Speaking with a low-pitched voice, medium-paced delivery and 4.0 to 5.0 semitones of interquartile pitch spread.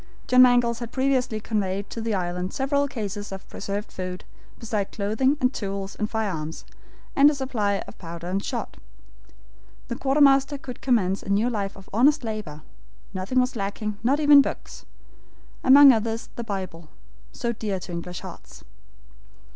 No: high, 215 Hz; average, 155 wpm; average, 4.6 semitones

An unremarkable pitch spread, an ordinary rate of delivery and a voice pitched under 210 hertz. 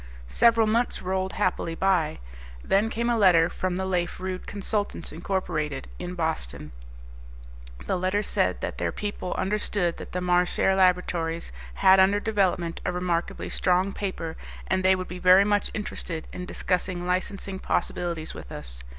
No: narrow, 2.0 semitones; average, 155 wpm; medium, 185 Hz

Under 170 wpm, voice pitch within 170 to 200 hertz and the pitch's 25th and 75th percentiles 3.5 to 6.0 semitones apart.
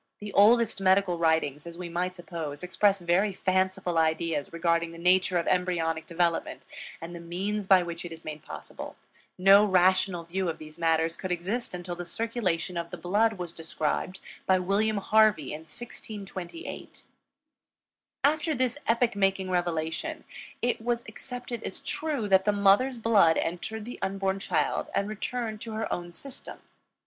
Yes: average, 160 wpm; medium, 185 Hz; average, 3.9 semitones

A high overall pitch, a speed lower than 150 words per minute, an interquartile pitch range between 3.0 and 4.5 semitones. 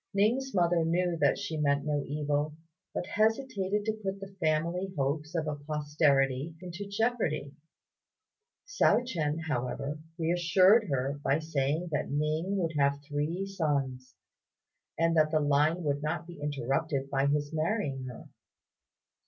No: medium, 155 Hz; average, 140 wpm; average, 3.9 semitones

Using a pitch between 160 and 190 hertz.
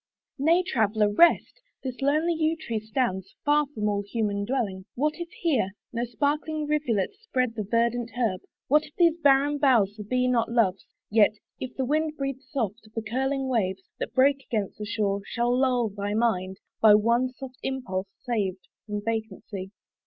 No: high, 240 Hz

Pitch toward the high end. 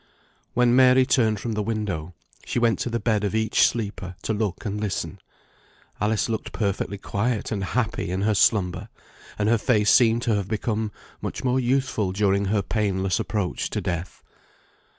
No: low, 105 Hz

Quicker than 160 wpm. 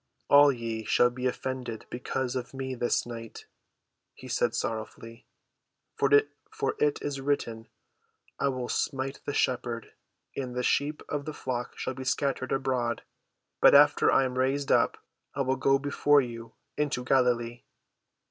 No: average, 145 wpm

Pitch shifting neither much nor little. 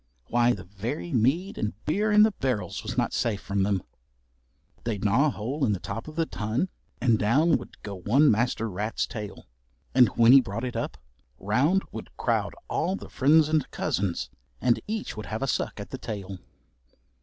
No: wide, 6.2 semitones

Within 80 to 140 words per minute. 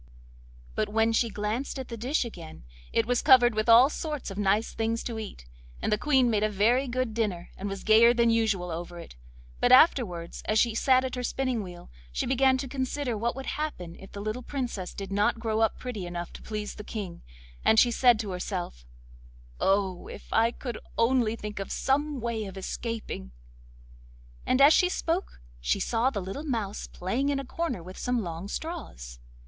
No: average, 195 wpm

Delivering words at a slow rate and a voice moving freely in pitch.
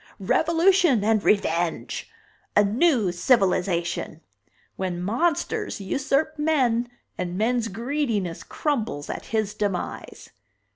Yes: slow, 95 wpm; wide, 7.0 semitones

